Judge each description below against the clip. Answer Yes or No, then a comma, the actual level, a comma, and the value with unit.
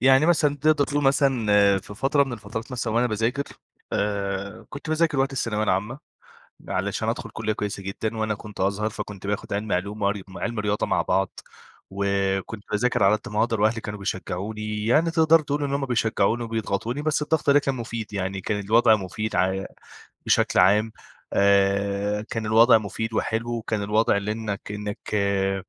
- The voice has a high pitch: No, low, 110 Hz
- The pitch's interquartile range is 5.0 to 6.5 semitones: No, average, 3.2 semitones